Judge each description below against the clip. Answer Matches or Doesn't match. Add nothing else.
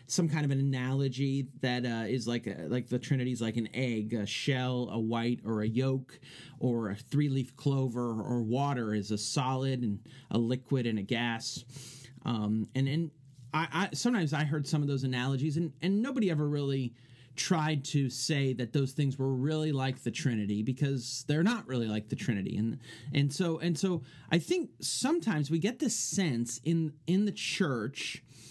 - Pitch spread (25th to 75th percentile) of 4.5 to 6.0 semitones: Doesn't match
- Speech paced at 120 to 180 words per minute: Doesn't match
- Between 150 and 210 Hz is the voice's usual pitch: Doesn't match